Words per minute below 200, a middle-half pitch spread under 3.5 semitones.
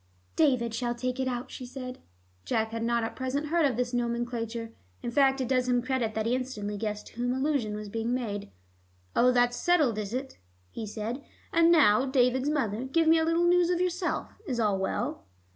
No: fast, 205 wpm; average, 3.0 semitones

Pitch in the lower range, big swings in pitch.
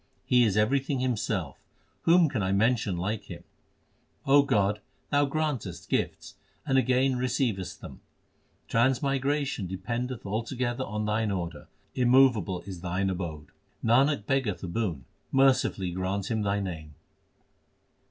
Yes: low, 110 Hz; wide, 5.7 semitones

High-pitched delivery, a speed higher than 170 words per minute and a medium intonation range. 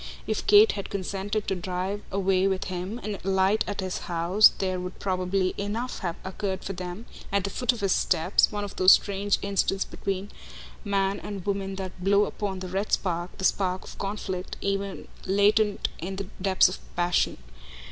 No: high, 195 Hz; average, 180 wpm; narrow, 1.5 semitones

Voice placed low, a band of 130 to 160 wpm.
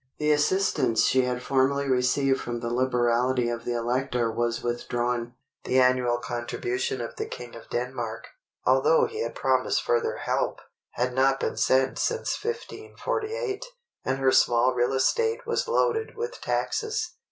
Yes: low, 130 Hz; average, 140 wpm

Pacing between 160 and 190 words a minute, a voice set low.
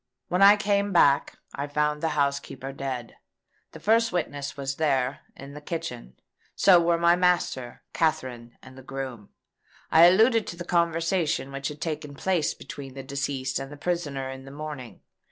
No: average, 170 wpm; medium, 145 Hz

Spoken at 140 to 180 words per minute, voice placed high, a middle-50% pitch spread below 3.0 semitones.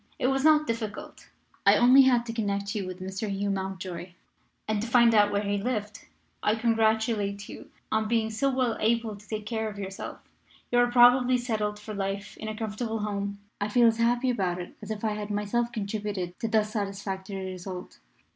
No: average, 195 wpm; high, 215 Hz; narrow, 2.5 semitones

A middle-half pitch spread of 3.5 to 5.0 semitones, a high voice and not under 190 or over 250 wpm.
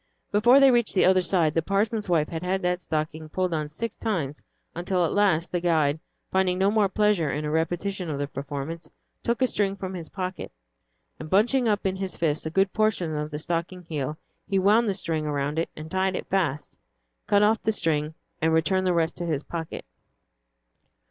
No: average, 3.9 semitones; medium, 175 Hz; fast, 205 wpm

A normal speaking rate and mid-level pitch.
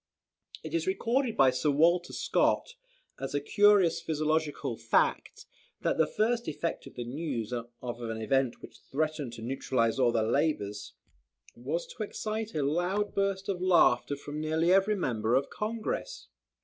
Yes: average, 160 wpm; medium, 155 Hz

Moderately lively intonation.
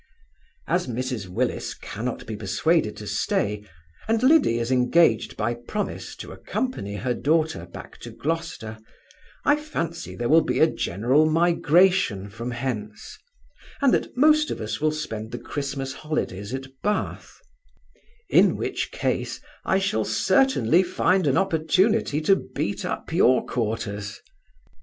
No: wide, 8.1 semitones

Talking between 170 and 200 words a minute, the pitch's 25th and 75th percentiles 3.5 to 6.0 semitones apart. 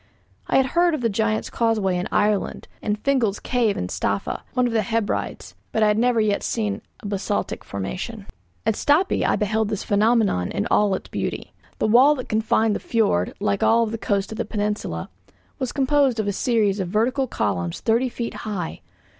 No: average, 190 wpm; average, 2.8 semitones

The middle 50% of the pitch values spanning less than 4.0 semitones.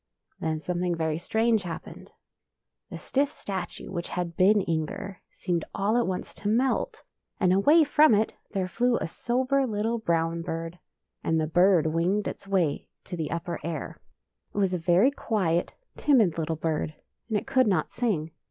No: average, 4.8 semitones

